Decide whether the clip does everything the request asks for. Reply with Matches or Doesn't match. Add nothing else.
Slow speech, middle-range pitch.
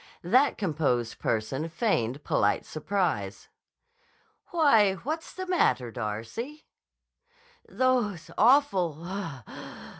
Matches